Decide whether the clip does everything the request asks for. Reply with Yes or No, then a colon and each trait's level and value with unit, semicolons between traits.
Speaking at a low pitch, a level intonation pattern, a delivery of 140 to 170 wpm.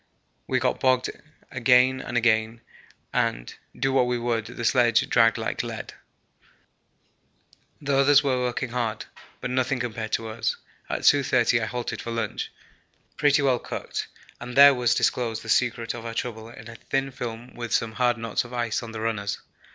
No: low, 120 Hz; narrow, 1.9 semitones; average, 180 wpm